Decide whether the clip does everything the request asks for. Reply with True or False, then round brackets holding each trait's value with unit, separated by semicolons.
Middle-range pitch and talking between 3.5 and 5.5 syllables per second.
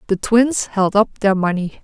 False (205 Hz; 4.3 syllables/s)